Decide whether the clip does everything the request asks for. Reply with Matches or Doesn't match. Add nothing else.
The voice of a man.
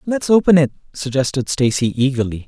Matches